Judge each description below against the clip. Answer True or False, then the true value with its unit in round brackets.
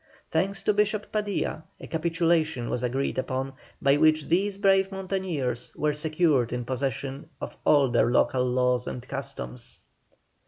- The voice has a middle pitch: True (150 Hz)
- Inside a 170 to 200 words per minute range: False (145 wpm)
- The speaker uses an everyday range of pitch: False (6.2 semitones)